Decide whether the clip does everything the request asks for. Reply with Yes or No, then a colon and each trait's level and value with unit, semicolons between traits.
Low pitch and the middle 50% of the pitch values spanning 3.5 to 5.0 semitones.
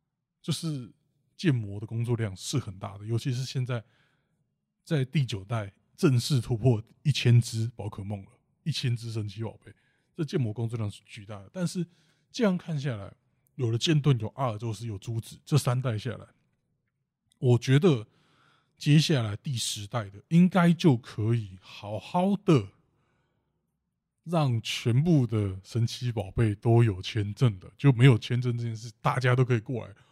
Yes: low, 125 Hz; average, 4.7 semitones